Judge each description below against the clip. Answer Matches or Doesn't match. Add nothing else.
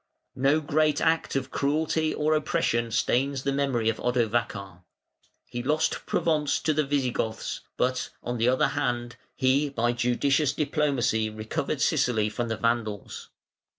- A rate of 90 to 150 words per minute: Matches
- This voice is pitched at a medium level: Doesn't match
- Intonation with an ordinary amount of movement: Matches